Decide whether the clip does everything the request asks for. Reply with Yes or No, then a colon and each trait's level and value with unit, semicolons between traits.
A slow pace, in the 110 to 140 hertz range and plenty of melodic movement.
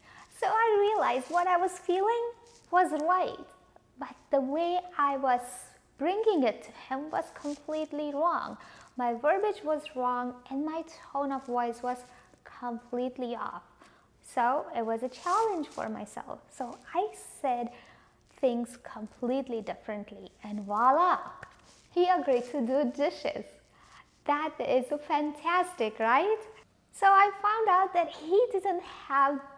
No: slow, 130 wpm; very high, 295 Hz; wide, 6.5 semitones